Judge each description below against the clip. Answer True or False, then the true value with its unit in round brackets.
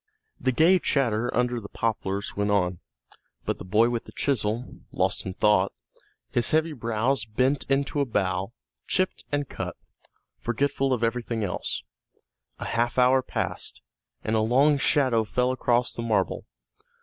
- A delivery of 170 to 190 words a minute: False (150 wpm)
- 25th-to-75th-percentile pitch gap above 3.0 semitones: True (3.8 semitones)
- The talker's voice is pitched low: True (120 Hz)